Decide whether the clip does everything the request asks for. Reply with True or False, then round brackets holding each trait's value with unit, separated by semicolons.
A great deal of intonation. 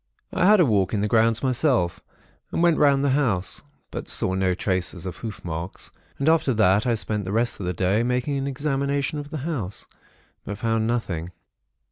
True (6.6 semitones)